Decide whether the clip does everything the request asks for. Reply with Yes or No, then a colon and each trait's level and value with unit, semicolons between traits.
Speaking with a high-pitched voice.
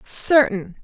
Yes: high, 235 Hz